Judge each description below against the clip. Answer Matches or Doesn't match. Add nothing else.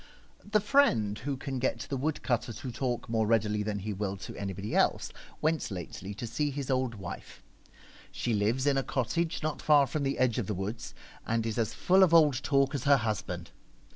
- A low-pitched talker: Matches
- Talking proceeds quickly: Matches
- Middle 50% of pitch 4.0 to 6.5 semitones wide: Matches